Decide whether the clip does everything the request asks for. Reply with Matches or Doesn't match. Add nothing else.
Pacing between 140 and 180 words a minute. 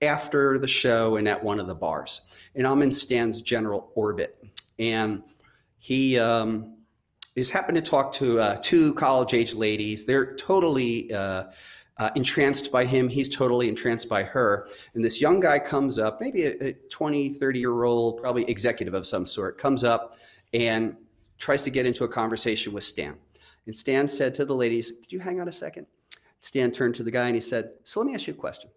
Doesn't match